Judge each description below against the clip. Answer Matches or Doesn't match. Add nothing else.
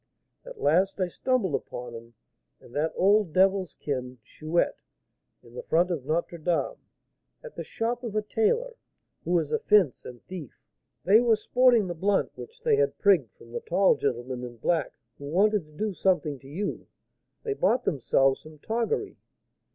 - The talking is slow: Doesn't match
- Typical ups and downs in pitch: Doesn't match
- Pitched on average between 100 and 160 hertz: Doesn't match